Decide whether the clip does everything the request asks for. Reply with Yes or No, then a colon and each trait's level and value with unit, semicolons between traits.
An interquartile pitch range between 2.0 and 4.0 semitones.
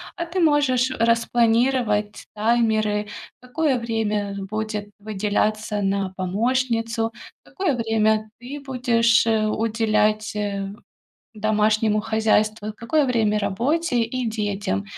Yes: narrow, 2.4 semitones